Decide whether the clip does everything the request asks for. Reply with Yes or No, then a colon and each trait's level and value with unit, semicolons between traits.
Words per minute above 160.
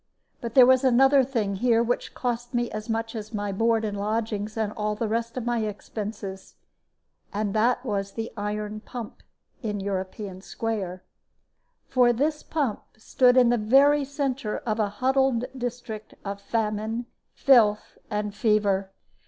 No: average, 150 wpm